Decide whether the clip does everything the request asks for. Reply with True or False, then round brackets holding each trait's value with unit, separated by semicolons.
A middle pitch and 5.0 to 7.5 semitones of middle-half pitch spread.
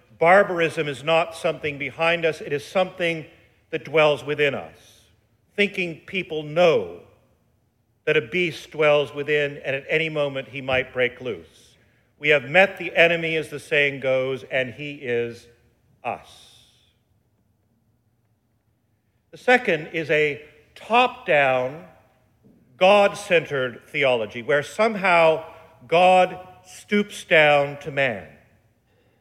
True (145 Hz; 5.6 semitones)